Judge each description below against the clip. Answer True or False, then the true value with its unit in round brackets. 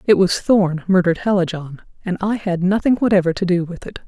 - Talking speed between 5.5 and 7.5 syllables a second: True (5.8 syllables/s)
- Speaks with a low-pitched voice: False (185 Hz)